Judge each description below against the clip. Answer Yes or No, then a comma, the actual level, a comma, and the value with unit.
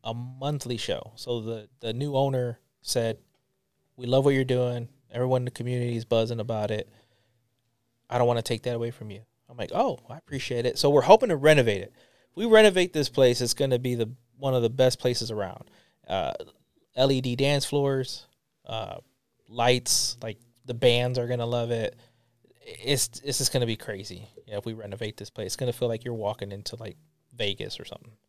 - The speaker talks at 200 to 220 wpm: Yes, fast, 205 wpm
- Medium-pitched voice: No, low, 120 Hz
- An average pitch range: No, narrow, 2.1 semitones